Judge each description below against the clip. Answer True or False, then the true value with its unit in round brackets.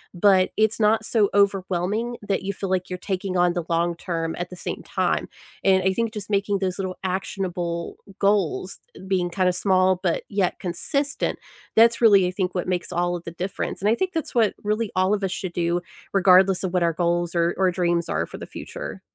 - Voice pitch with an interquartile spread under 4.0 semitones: True (2.4 semitones)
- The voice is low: False (185 Hz)